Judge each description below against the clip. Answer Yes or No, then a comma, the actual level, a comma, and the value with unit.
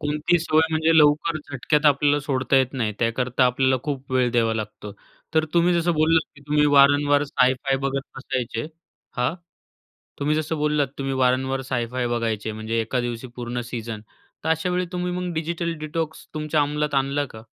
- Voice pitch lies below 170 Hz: Yes, medium, 140 Hz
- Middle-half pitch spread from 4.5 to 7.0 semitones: No, average, 3.6 semitones